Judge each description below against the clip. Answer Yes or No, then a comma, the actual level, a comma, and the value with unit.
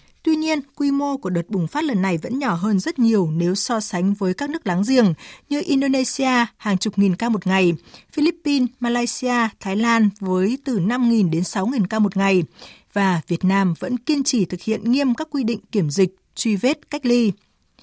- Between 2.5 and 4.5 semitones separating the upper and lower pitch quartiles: No, average, 5.2 semitones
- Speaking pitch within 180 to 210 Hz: No, high, 220 Hz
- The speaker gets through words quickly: No, average, 205 wpm